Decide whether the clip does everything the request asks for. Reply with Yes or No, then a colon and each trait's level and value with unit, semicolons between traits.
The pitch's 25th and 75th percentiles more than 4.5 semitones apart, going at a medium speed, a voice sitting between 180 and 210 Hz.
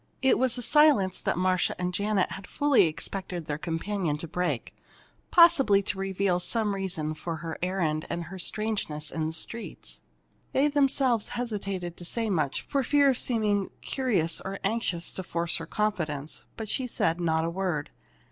Yes: average, 5.2 semitones; average, 170 wpm; high, 190 Hz